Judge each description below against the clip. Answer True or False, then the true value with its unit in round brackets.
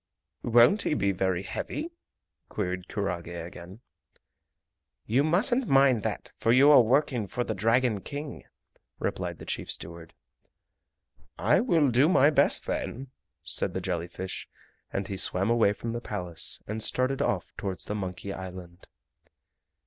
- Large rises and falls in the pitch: True (6.4 semitones)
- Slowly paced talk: False (145 wpm)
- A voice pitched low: True (110 Hz)